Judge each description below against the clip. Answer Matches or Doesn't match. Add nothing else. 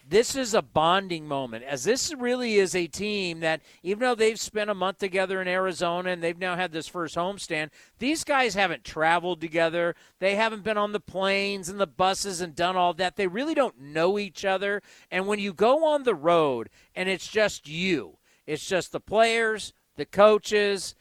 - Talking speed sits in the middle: Matches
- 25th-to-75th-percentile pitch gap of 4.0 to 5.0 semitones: Doesn't match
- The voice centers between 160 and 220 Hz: Matches